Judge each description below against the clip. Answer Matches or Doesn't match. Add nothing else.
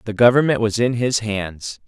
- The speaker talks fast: Doesn't match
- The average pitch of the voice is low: Matches